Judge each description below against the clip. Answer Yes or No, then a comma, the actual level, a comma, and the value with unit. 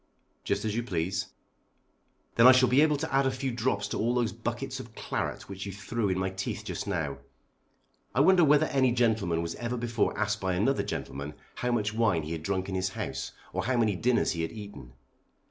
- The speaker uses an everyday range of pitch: Yes, average, 4.9 semitones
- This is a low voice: Yes, low, 110 Hz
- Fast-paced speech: Yes, fast, 215 wpm